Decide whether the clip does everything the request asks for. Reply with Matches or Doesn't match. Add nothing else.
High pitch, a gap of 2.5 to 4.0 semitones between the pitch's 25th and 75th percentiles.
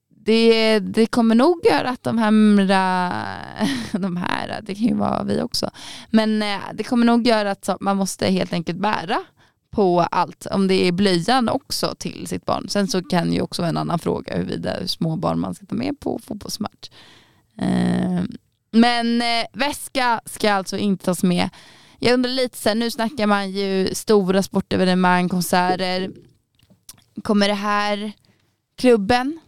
Matches